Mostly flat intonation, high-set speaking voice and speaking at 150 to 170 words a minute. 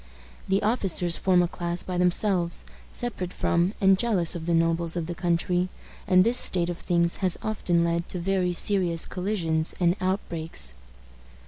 No: narrow, 1.9 semitones; medium, 175 Hz; average, 160 wpm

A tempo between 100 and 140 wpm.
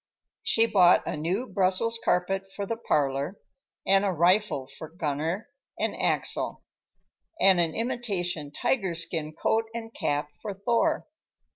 Yes: slow, 135 wpm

